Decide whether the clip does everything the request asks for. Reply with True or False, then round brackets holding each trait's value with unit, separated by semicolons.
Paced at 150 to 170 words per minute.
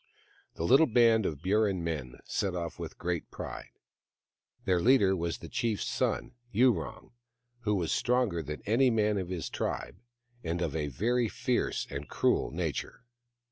True (155 wpm)